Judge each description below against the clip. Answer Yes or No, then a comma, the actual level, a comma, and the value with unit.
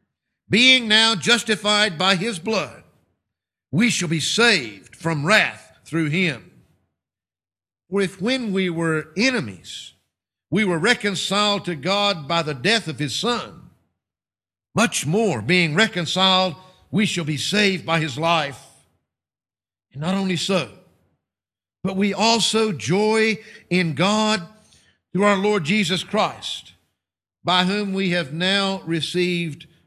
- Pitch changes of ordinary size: No, wide, 5.8 semitones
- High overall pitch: No, medium, 180 Hz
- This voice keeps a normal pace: No, slow, 125 wpm